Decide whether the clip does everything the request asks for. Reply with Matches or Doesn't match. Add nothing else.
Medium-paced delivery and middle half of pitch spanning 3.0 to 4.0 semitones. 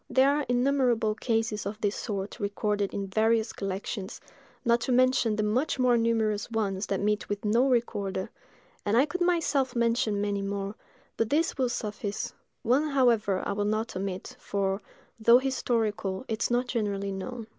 Matches